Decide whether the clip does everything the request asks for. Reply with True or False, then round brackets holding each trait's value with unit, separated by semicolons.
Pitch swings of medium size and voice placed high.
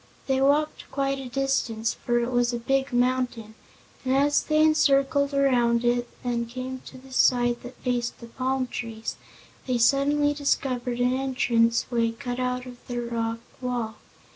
False (2.2 semitones; 250 Hz)